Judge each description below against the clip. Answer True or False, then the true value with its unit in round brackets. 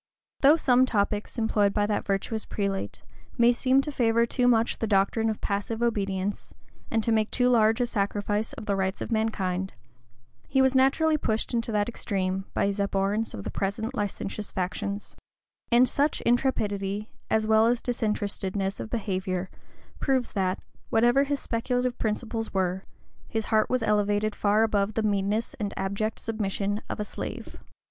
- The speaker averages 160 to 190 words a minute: True (165 wpm)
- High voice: True (215 Hz)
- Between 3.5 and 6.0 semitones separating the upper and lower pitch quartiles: False (2.8 semitones)